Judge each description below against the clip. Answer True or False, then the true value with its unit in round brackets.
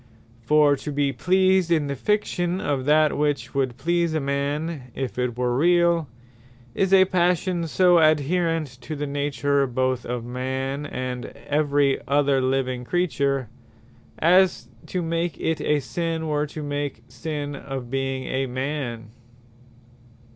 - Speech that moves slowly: False (145 wpm)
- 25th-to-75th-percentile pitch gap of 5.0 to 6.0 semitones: False (3.9 semitones)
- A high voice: False (145 Hz)